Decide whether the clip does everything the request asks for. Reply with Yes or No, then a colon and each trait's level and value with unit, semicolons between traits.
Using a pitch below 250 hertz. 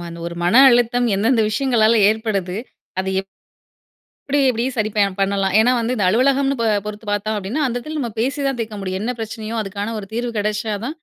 Yes: high, 220 Hz